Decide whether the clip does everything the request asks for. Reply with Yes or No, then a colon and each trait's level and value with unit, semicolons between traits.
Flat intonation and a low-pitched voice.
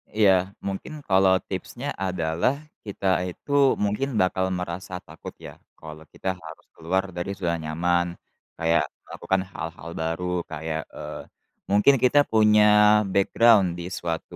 No: average, 3.5 semitones; very low, 90 Hz